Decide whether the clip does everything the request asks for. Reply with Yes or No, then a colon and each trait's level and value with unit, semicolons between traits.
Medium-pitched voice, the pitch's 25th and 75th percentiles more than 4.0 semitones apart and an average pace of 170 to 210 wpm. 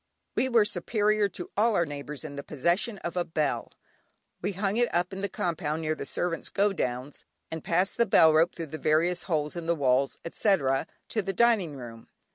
Yes: medium, 170 Hz; average, 4.8 semitones; average, 200 wpm